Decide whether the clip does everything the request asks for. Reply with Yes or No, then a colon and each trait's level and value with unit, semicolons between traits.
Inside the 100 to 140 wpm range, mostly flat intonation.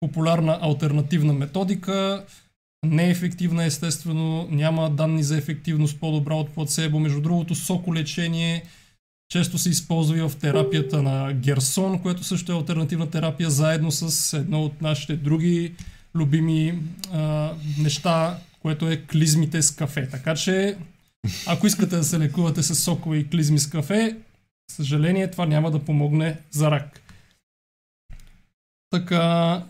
Yes: average, 130 wpm; narrow, 2.0 semitones